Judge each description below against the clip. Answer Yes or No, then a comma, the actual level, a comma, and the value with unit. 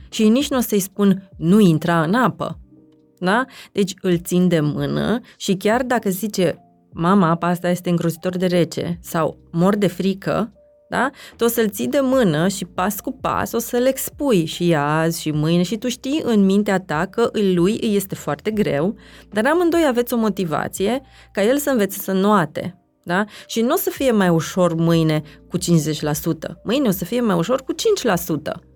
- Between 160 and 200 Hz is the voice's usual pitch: Yes, high, 190 Hz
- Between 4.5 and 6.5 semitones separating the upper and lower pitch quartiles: Yes, average, 5.2 semitones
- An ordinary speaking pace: No, fast, 190 wpm